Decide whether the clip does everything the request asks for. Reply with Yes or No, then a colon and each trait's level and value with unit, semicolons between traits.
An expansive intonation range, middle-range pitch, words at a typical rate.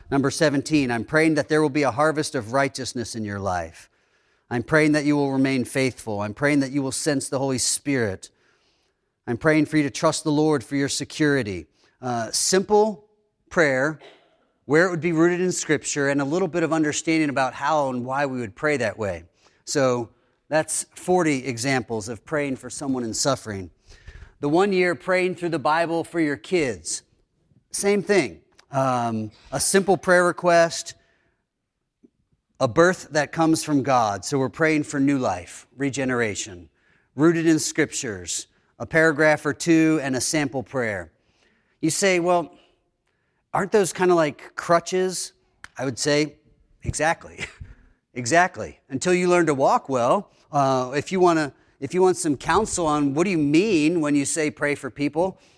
No: average, 4.1 semitones; medium, 145 Hz; average, 170 wpm